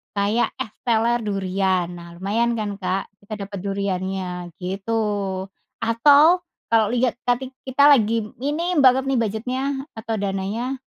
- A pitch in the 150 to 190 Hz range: No, high, 220 Hz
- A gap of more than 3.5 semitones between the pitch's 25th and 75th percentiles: Yes, average, 3.9 semitones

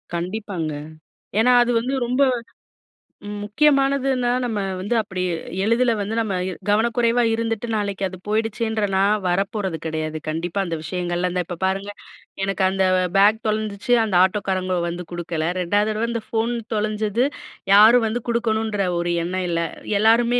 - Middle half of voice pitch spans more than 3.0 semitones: Yes, average, 3.7 semitones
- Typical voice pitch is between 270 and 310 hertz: No, high, 210 Hz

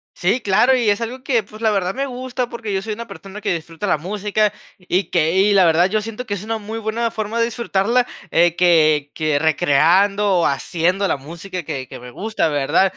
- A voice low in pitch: No, high, 195 Hz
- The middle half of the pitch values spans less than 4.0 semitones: No, average, 4.6 semitones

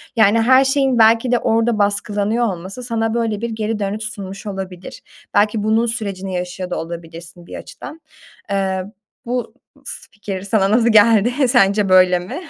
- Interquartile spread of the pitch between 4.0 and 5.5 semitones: No, average, 3.2 semitones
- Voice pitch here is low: No, high, 210 Hz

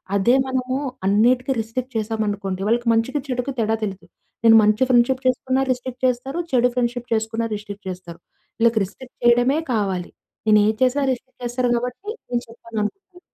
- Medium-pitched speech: No, high, 240 Hz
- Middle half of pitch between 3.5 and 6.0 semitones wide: No, average, 2.9 semitones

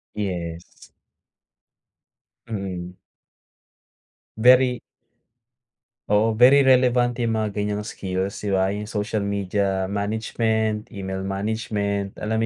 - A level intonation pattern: Yes, narrow, 2.3 semitones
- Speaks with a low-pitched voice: Yes, low, 105 Hz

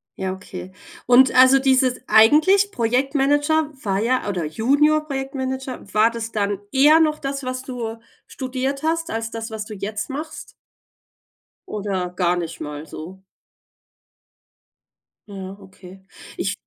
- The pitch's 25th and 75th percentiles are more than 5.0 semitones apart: Yes, wide, 5.5 semitones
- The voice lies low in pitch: No, high, 245 Hz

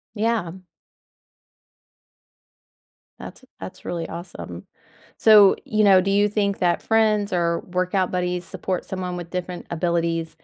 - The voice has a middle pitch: Yes, medium, 180 Hz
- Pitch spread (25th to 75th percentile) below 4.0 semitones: Yes, average, 2.8 semitones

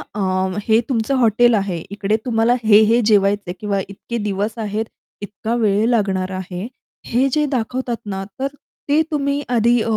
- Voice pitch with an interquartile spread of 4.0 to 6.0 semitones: No, average, 3.2 semitones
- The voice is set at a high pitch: Yes, high, 220 Hz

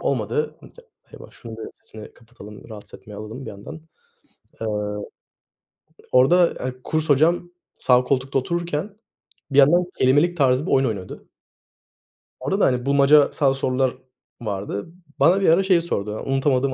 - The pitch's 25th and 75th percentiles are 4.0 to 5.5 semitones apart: Yes, average, 5.0 semitones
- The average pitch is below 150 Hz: Yes, low, 135 Hz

